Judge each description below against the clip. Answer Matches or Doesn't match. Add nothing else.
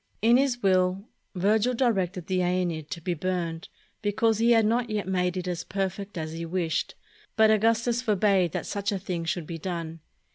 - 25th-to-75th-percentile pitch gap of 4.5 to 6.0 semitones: Doesn't match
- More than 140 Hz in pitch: Matches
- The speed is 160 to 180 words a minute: Doesn't match